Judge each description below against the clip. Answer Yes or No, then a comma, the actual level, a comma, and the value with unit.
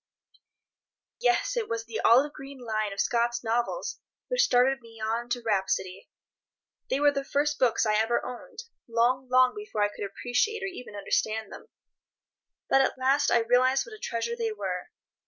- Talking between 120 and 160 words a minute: No, average, 170 wpm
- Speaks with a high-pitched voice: Yes, high, 245 Hz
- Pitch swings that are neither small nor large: Yes, average, 4.1 semitones